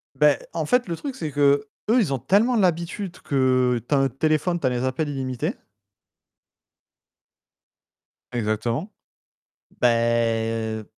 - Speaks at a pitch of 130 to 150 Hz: Yes, low, 135 Hz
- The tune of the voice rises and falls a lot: Yes, wide, 6.4 semitones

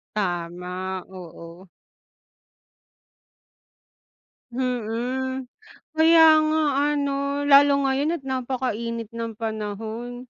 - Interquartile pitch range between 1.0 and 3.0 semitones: No, average, 4.6 semitones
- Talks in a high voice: Yes, high, 235 Hz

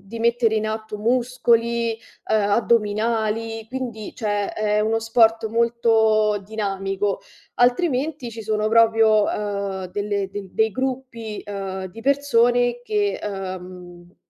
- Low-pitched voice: No, high, 220 Hz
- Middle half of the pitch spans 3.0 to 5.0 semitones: No, narrow, 2.4 semitones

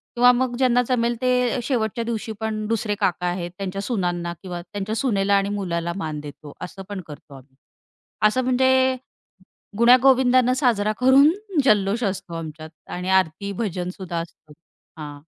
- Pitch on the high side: Yes, high, 205 Hz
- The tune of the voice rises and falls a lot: Yes, wide, 5.9 semitones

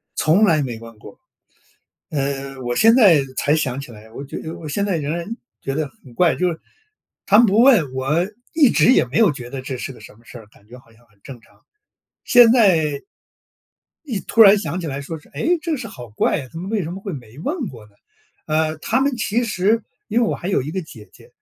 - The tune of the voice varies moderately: No, wide, 7.9 semitones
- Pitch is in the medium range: Yes, medium, 155 Hz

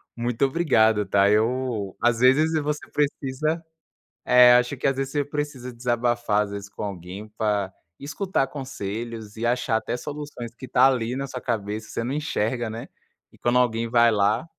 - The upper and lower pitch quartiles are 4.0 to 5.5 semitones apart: No, average, 3.5 semitones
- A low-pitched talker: Yes, low, 120 Hz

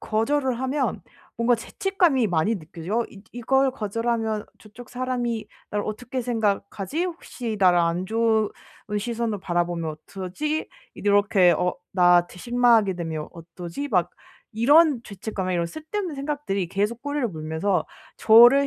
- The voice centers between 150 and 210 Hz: No, high, 220 Hz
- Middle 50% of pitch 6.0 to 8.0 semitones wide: No, average, 5.3 semitones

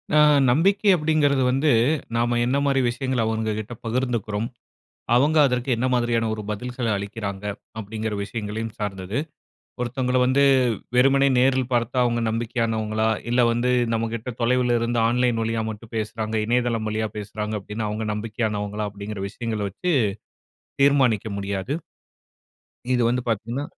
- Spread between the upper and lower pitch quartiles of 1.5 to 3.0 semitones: Yes, narrow, 2.6 semitones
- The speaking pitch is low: Yes, low, 115 Hz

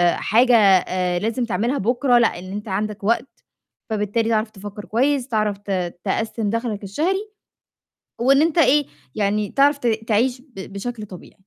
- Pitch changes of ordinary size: Yes, average, 3.7 semitones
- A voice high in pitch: Yes, high, 220 Hz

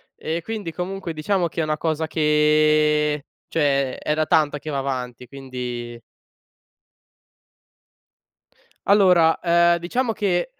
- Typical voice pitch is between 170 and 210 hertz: No, medium, 155 Hz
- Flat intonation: No, average, 3.1 semitones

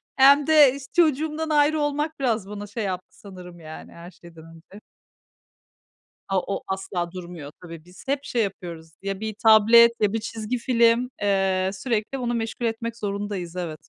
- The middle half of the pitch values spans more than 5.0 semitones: Yes, wide, 5.4 semitones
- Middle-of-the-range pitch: No, high, 210 Hz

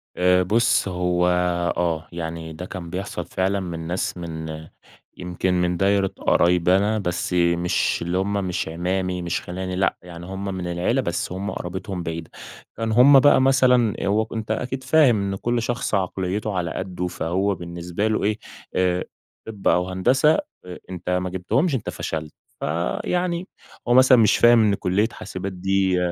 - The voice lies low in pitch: Yes, very low, 95 Hz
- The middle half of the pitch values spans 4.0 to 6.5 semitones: No, average, 3.4 semitones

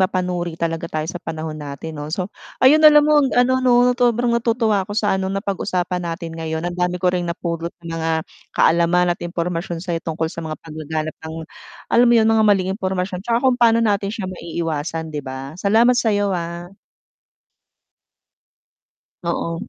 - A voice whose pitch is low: No, medium, 180 Hz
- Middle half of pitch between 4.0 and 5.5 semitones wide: Yes, average, 4.5 semitones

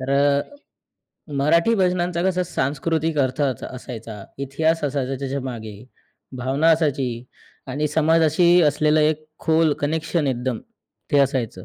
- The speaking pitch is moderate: Yes, medium, 145 Hz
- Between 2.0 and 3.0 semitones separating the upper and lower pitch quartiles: No, average, 3.5 semitones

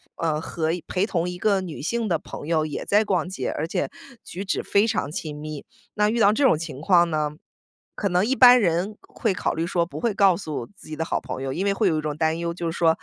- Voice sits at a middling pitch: Yes, medium, 170 Hz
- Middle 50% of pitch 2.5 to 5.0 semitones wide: Yes, average, 4.2 semitones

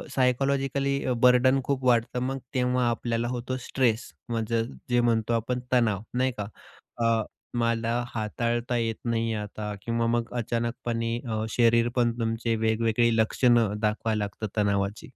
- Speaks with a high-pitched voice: No, low, 115 Hz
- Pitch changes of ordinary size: No, narrow, 1.8 semitones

